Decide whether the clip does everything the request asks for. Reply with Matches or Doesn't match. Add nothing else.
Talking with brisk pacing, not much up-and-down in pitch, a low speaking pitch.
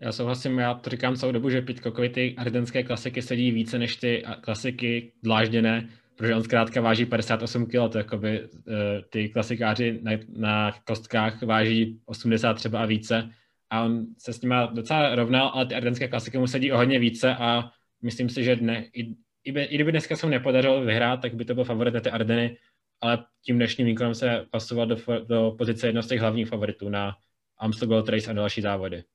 Matches